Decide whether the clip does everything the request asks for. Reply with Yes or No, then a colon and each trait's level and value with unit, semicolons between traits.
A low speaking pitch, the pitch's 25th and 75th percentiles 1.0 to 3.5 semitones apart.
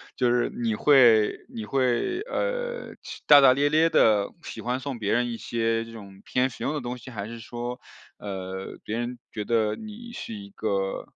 No: low, 120 Hz; average, 4.0 semitones